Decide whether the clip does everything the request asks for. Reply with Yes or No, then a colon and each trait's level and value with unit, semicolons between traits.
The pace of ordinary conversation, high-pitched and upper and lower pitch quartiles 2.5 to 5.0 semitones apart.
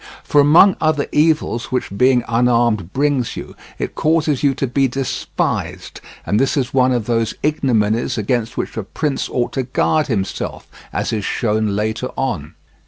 No: average, 165 wpm; low, 125 Hz; average, 4.2 semitones